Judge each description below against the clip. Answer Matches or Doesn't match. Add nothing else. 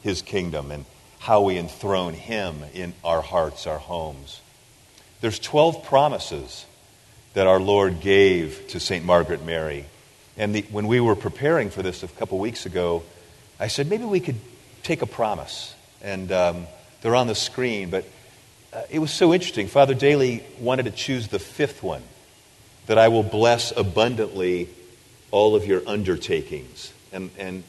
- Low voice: Matches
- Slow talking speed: Doesn't match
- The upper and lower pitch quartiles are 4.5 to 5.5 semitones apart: Matches